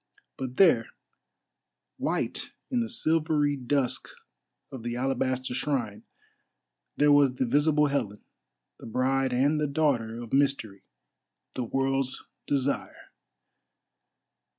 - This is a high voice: No, low, 135 Hz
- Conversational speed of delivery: No, slow, 105 wpm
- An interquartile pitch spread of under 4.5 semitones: Yes, narrow, 2.6 semitones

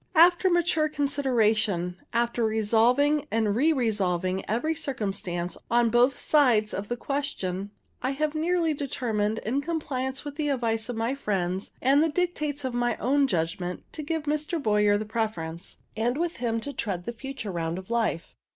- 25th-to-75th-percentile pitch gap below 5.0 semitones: No, wide, 5.6 semitones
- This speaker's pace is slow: No, average, 165 wpm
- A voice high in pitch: Yes, high, 240 Hz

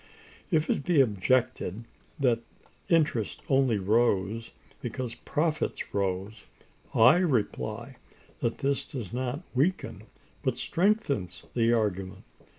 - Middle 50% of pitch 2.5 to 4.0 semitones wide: No, average, 5.1 semitones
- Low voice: Yes, low, 125 Hz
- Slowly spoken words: Yes, slow, 105 wpm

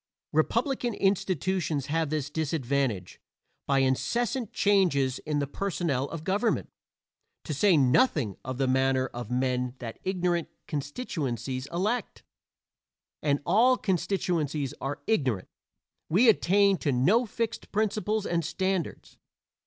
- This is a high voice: No, medium, 160 Hz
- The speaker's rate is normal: No, slow, 115 wpm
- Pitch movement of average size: No, wide, 6.8 semitones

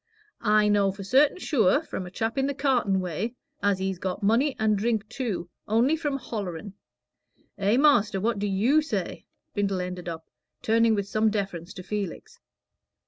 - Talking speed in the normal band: Yes, average, 165 wpm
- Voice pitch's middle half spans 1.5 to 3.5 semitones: No, average, 4.0 semitones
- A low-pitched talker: No, high, 210 Hz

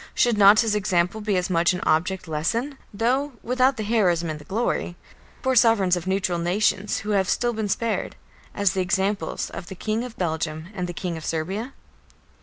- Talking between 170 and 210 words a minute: Yes, average, 195 wpm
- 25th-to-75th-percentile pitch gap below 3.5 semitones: No, average, 4.2 semitones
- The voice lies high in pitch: Yes, high, 195 Hz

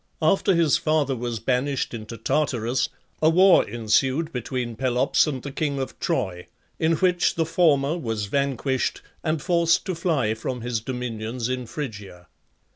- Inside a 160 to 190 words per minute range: No, average, 150 wpm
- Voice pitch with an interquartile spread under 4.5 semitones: No, average, 5.1 semitones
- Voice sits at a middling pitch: No, low, 130 Hz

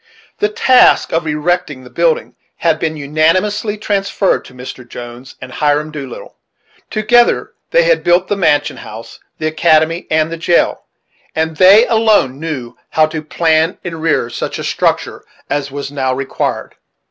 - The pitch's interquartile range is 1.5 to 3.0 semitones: No, average, 4.8 semitones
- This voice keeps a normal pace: Yes, average, 155 wpm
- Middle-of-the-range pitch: Yes, medium, 160 Hz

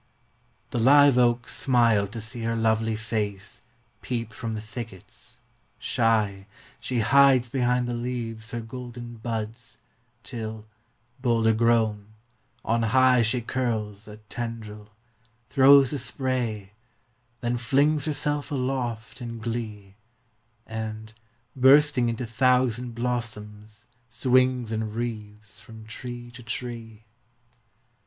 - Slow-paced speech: Yes, slow, 115 wpm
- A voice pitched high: No, low, 115 Hz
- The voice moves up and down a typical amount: No, narrow, 2.3 semitones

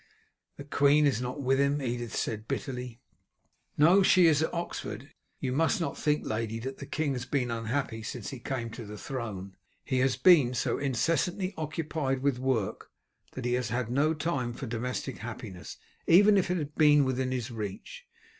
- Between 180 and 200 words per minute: Yes, average, 185 wpm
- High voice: No, low, 130 Hz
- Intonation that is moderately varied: Yes, average, 4.0 semitones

